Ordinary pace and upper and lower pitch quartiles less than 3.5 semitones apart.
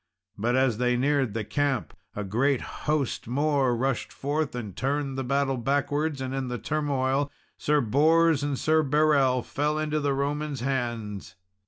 Yes: average, 160 wpm; average, 2.9 semitones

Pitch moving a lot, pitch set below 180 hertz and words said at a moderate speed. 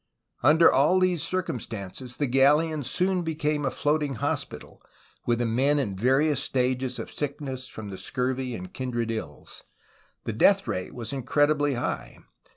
No: average, 3.7 semitones; low, 135 Hz; average, 155 wpm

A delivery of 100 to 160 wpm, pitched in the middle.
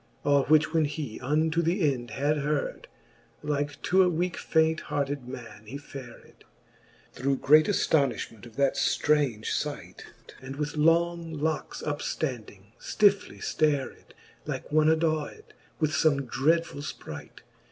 Yes: average, 140 wpm; medium, 150 Hz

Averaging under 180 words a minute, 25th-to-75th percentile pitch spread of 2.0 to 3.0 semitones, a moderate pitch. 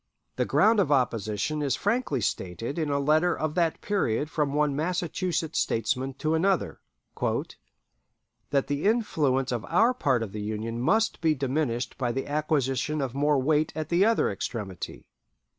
No: average, 160 wpm; average, 4.3 semitones; medium, 145 Hz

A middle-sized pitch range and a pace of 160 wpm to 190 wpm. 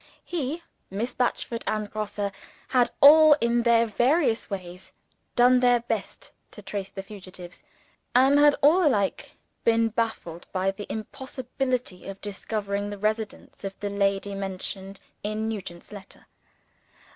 No: average, 3.9 semitones; slow, 135 wpm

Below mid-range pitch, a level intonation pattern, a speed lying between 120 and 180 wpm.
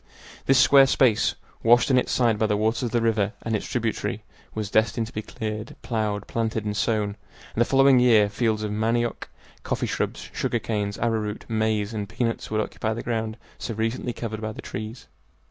No: low, 110 Hz; narrow, 1.6 semitones; average, 195 wpm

